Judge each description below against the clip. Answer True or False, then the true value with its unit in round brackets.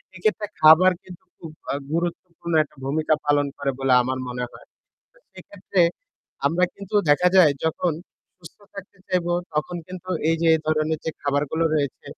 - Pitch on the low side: False (160 Hz)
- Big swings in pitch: False (3.7 semitones)